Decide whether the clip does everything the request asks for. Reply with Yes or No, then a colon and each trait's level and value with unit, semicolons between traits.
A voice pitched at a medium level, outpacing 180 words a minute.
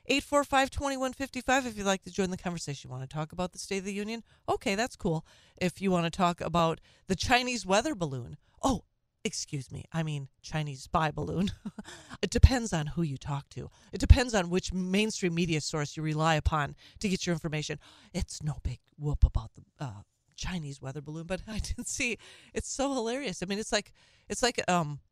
Yes: medium, 175 Hz; fast, 205 wpm